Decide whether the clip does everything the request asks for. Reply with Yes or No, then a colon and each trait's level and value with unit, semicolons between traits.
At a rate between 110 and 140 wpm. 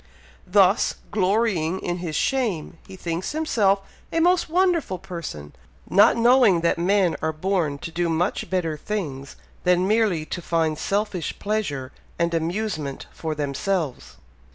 Yes: slow, 135 wpm